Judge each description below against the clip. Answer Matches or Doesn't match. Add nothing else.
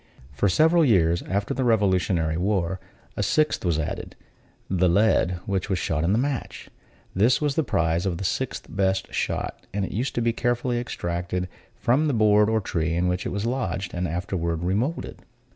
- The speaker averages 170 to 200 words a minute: Matches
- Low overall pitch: Matches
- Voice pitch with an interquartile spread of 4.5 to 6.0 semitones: Matches